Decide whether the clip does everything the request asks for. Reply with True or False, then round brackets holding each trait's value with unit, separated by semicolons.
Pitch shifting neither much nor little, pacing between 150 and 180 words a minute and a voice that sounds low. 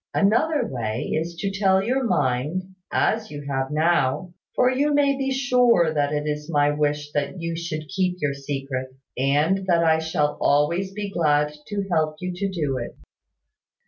False (4.9 semitones; 175 wpm; 160 Hz)